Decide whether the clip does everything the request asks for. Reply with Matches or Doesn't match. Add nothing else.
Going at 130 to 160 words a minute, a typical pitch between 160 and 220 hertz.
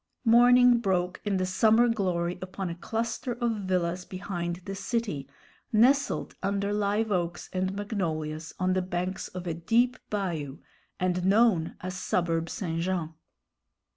Matches